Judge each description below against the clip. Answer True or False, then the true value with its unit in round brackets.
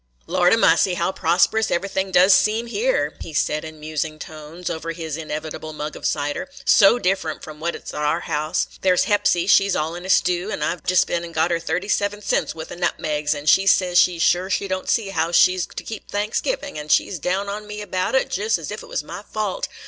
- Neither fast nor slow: False (245 wpm)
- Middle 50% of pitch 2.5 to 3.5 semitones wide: False (3.9 semitones)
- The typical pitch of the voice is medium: True (180 Hz)